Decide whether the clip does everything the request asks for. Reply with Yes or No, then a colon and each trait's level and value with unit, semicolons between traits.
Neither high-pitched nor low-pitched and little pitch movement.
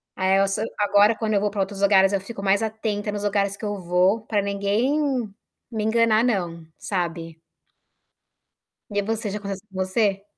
No: high, 200 Hz; narrow, 1.8 semitones